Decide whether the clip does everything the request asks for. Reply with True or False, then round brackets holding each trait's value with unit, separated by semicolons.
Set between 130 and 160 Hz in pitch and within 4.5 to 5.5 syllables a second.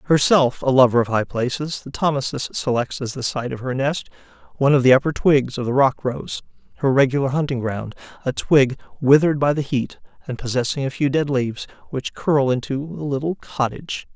True (135 Hz; 5.4 syllables/s)